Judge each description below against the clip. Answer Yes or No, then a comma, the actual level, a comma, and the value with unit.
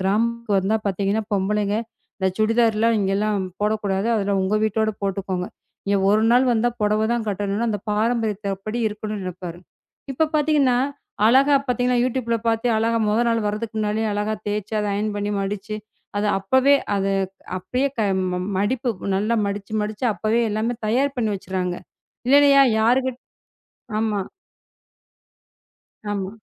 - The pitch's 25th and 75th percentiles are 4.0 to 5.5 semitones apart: No, narrow, 2.6 semitones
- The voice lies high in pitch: Yes, high, 215 Hz